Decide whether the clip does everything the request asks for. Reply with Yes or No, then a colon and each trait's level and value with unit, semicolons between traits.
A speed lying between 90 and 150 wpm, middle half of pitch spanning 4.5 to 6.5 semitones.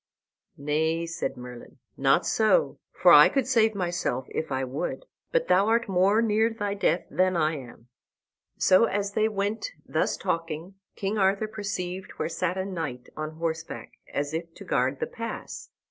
No: average, 165 wpm; average, 4.9 semitones